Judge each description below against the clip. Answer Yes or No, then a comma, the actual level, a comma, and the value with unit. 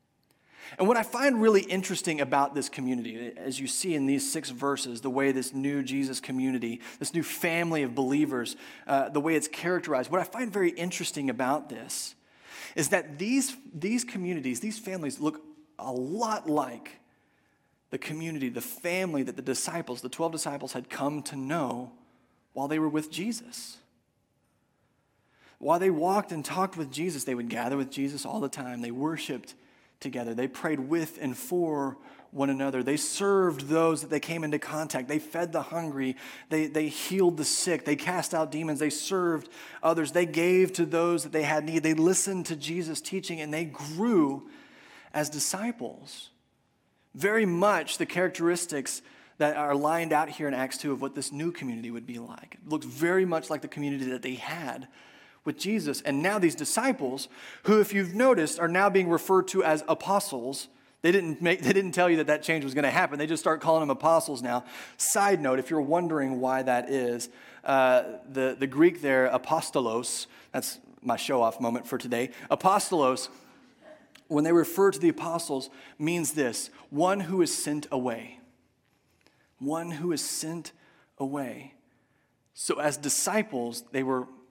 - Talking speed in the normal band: Yes, average, 175 wpm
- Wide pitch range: No, average, 4.7 semitones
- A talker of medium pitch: Yes, medium, 155 Hz